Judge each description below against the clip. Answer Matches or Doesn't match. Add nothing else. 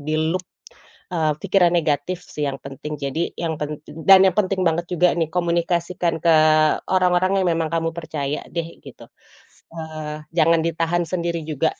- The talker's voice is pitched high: Doesn't match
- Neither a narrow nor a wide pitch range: Doesn't match